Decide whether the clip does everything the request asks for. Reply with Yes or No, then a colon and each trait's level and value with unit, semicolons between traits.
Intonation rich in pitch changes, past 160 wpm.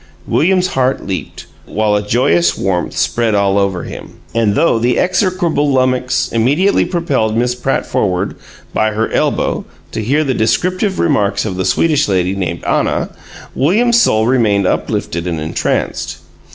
No: wide, 6.8 semitones; average, 150 wpm